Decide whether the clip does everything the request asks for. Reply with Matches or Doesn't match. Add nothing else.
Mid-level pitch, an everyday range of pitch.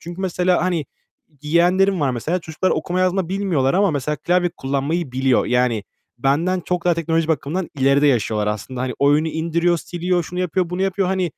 Matches